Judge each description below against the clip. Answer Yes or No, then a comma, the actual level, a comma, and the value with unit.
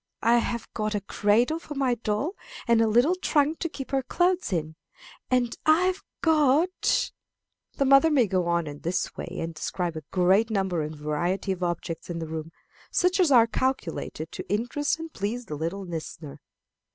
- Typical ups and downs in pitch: No, wide, 8.2 semitones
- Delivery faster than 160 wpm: Yes, average, 190 wpm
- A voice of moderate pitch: No, high, 220 Hz